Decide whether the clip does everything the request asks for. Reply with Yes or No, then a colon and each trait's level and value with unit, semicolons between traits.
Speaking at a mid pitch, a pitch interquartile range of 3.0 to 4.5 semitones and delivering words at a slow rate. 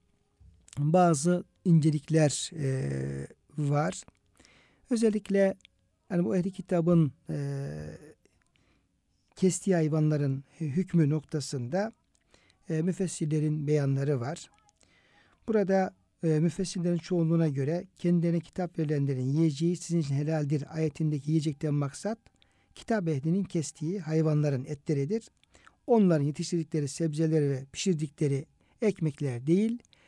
Yes: medium, 160 Hz; average, 3.6 semitones; slow, 90 wpm